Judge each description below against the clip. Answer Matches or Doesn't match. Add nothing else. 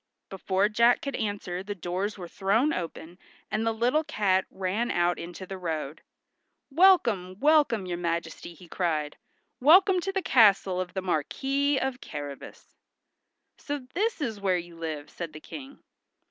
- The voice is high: Matches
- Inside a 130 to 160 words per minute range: Matches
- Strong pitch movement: Matches